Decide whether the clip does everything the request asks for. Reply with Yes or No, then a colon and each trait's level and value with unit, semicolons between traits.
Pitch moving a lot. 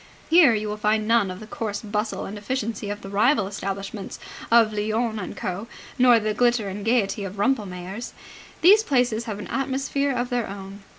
No: average, 3.1 semitones